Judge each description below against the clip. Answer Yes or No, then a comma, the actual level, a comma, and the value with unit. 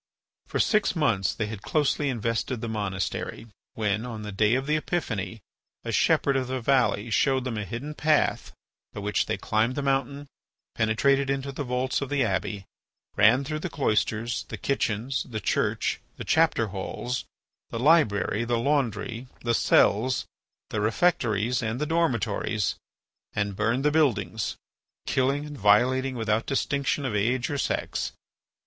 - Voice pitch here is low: Yes, low, 120 Hz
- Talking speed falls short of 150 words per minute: No, average, 155 wpm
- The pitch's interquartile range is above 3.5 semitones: Yes, average, 4.3 semitones